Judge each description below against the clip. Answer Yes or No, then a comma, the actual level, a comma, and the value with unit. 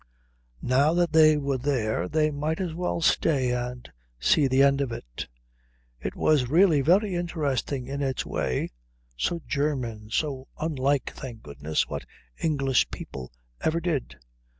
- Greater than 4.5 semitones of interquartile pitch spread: No, average, 4.1 semitones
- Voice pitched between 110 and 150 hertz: Yes, medium, 140 Hz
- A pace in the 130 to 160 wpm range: Yes, average, 145 wpm